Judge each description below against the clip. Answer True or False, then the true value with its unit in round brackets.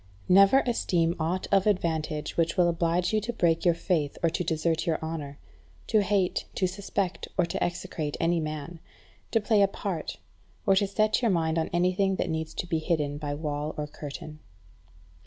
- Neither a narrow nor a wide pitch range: True (3.3 semitones)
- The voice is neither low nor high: True (170 Hz)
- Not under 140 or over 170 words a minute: False (190 wpm)